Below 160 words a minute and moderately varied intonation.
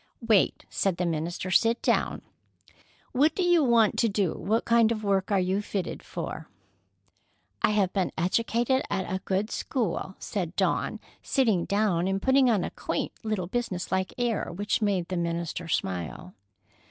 No: average, 165 wpm; average, 4.1 semitones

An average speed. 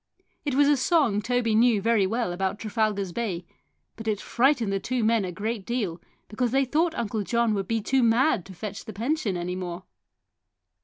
Yes: average, 195 wpm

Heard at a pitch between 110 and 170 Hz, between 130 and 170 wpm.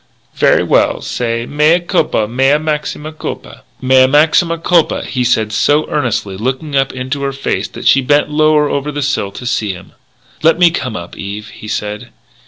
No: low, 135 Hz; average, 180 wpm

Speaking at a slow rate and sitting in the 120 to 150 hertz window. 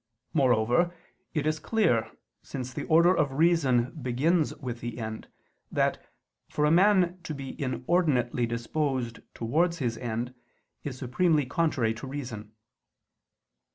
Yes: slow, 125 wpm; low, 135 Hz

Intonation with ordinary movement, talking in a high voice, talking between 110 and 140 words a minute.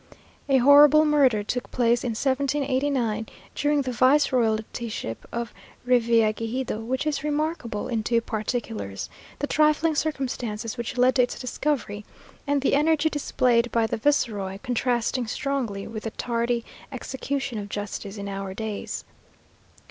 Yes: average, 4.0 semitones; high, 245 Hz; slow, 135 wpm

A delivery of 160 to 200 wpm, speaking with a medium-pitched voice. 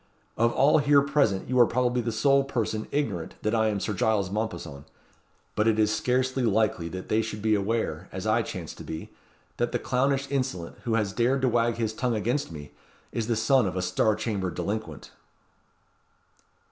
No: average, 190 wpm; low, 110 Hz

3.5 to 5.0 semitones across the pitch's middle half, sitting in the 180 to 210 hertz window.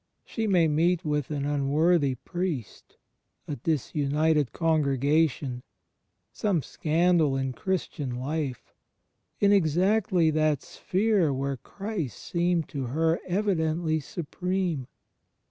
No: average, 4.0 semitones; medium, 160 Hz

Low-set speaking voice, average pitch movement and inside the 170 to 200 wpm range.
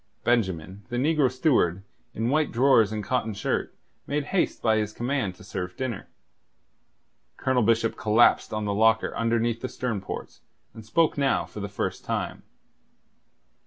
No: low, 115 Hz; average, 3.8 semitones; average, 155 wpm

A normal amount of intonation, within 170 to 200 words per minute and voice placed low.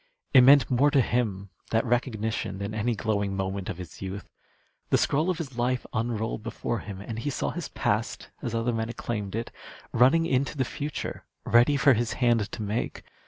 Yes: average, 3.6 semitones; average, 190 wpm; low, 115 Hz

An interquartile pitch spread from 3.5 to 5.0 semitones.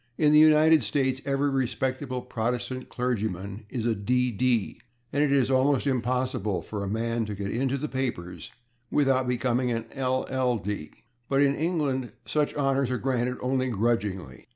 No: average, 3.0 semitones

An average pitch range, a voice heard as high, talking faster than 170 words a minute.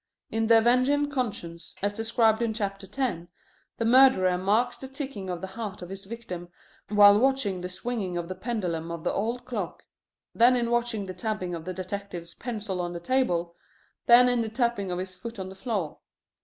Yes: average, 4.5 semitones; high, 205 Hz; average, 195 wpm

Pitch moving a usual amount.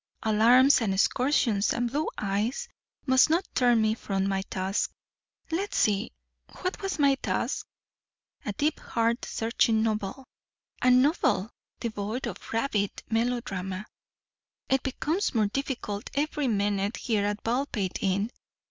Yes: average, 4.6 semitones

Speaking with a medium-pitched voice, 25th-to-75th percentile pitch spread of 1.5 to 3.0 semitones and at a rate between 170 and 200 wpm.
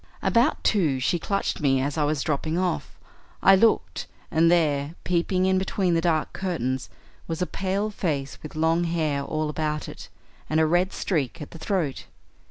No: medium, 165 Hz; average, 3.7 semitones; average, 175 wpm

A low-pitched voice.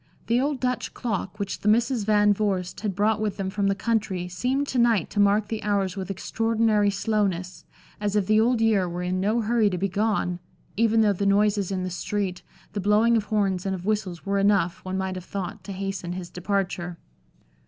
No: high, 205 Hz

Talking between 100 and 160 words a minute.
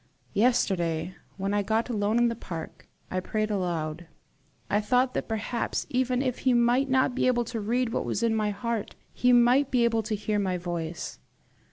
No: average, 190 wpm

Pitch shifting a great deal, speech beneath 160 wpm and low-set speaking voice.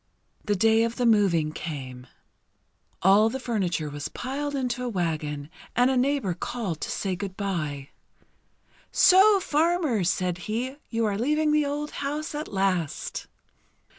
No: wide, 7.7 semitones; average, 145 wpm; high, 220 Hz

